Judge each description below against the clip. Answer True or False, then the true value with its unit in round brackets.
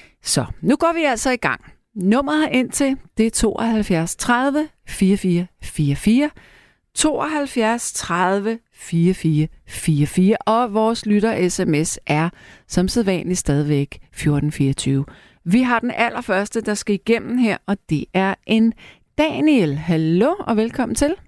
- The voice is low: False (210 Hz)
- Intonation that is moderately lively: False (5.9 semitones)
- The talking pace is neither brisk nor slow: False (125 wpm)